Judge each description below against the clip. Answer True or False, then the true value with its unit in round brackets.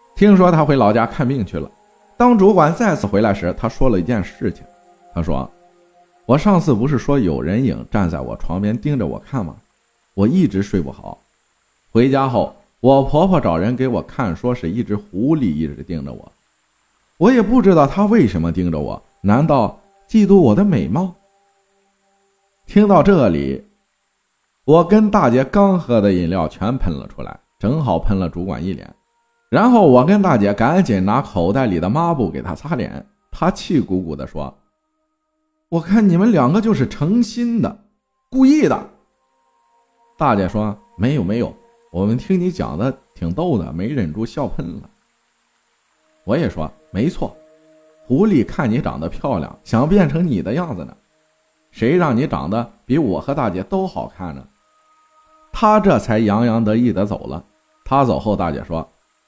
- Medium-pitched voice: True (155 Hz)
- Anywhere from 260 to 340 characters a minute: False (235 characters per minute)